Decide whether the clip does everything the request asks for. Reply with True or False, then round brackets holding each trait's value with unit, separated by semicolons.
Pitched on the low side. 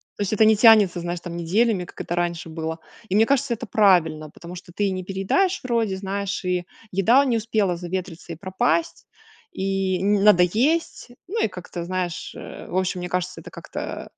False (190 Hz)